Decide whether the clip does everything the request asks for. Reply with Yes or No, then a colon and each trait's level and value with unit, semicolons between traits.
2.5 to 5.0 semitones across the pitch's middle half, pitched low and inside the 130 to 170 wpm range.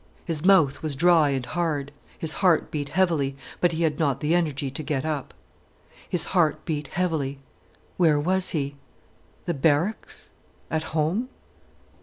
No: average, 3.2 semitones; medium, 155 Hz; average, 140 wpm